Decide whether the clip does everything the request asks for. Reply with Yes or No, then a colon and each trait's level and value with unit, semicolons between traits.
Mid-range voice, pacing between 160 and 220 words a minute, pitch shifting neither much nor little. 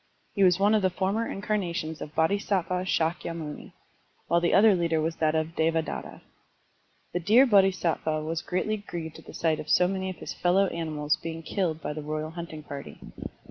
Yes: medium, 170 Hz; average, 180 wpm; average, 3.1 semitones